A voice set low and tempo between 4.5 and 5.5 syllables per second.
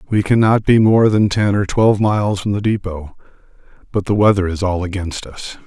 Yes: low, 100 Hz; 5.4 syllables/s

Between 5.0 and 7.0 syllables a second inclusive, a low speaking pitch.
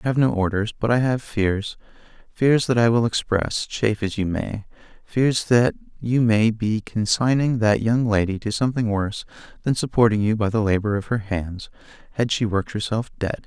Yes: 5.1 syllables/s; low, 110 Hz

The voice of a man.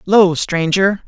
Yes: male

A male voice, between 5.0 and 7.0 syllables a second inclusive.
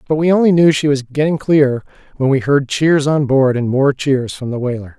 Yes: male; 5.1 syllables/s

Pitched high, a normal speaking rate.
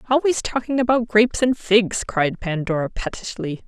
Yes: high, 215 Hz; average, 145 wpm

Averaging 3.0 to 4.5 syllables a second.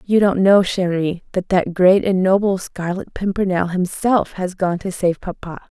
Yes: 4.4 syllables/s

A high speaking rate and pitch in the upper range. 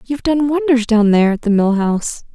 Yes: fast, 230 wpm; high, 240 Hz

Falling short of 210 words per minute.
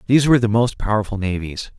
Yes: average, 200 wpm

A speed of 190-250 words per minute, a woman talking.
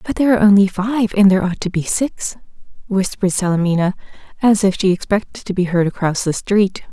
Yes: average, 200 wpm; female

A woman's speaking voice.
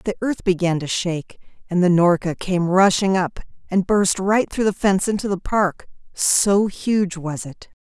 Yes: female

